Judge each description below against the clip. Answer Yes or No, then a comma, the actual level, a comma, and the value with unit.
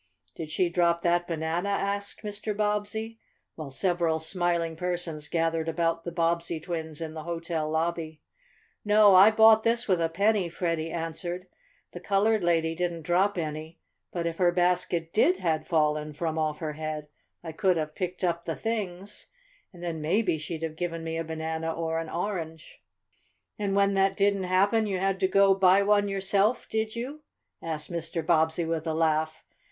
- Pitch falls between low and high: Yes, medium, 170 Hz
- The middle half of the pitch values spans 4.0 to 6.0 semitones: No, average, 3.3 semitones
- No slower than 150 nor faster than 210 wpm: Yes, average, 175 wpm